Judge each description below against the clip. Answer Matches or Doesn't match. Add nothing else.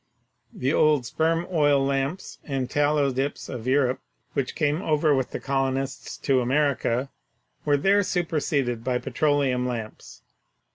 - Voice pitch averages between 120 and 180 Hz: Matches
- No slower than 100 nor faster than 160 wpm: Matches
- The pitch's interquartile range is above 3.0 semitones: Doesn't match